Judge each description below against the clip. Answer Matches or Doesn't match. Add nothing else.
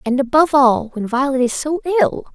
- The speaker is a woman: Matches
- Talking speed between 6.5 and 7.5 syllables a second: Doesn't match